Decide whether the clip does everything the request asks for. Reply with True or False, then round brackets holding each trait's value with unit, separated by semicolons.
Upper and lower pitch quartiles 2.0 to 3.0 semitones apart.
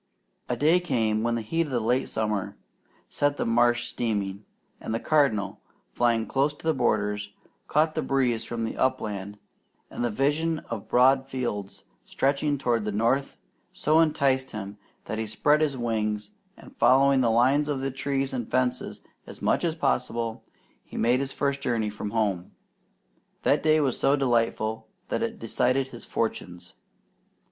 False (3.9 semitones)